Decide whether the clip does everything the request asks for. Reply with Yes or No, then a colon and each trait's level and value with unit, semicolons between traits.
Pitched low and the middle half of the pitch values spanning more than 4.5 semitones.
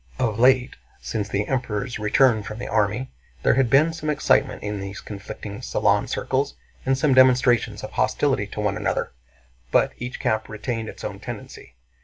No: low, 120 Hz; average, 3.8 semitones